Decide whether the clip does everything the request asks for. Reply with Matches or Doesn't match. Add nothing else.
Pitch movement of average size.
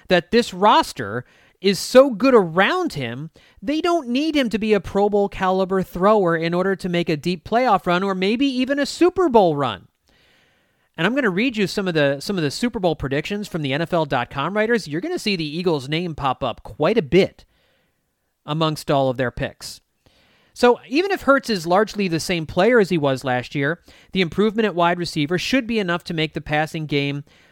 Doesn't match